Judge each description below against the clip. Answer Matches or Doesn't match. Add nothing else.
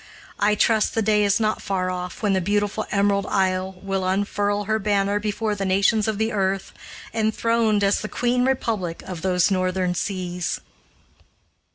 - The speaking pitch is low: Doesn't match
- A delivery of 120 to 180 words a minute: Matches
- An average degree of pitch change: Doesn't match